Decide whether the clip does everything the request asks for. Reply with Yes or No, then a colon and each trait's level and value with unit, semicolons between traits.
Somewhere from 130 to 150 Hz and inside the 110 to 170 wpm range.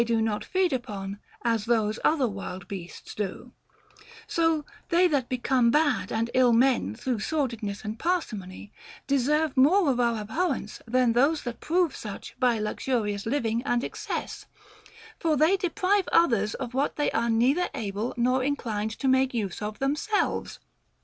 No: high, 245 Hz; average, 160 wpm